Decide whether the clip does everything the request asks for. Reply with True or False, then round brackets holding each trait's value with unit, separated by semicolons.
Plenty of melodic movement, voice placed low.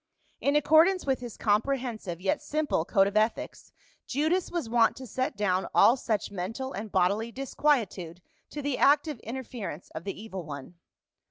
False (6.0 semitones; 230 Hz)